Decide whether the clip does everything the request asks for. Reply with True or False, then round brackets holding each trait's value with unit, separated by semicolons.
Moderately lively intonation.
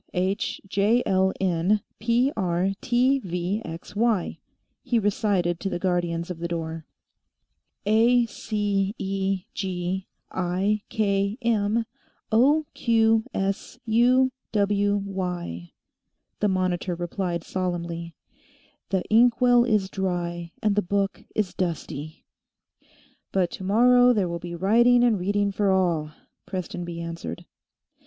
True (3.8 semitones)